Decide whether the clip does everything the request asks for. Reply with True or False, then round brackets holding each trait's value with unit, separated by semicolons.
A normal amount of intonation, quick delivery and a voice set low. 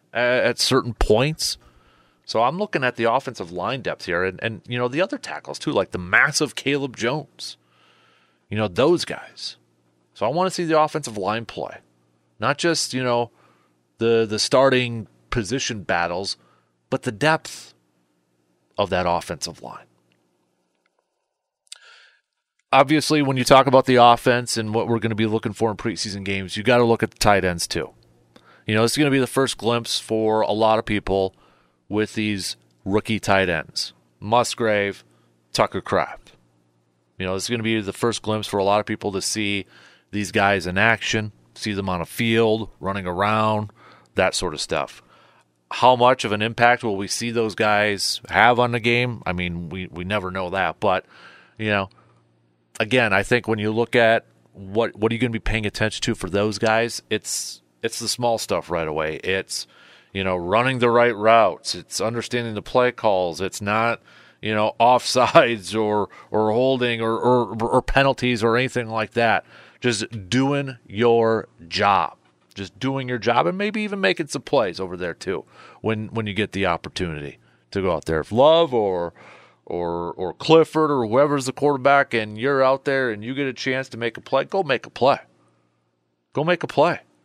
False (4.8 semitones; 190 wpm; 110 Hz)